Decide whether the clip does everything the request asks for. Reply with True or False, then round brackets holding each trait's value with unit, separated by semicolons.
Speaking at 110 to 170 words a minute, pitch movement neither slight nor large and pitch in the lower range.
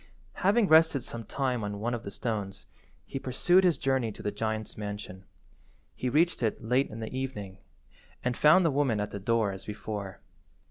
False (185 wpm; 4.7 semitones; 115 Hz)